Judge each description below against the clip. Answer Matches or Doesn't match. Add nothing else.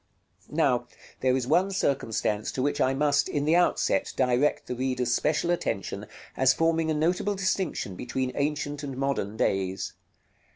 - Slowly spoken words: Doesn't match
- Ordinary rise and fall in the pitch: Matches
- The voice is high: Doesn't match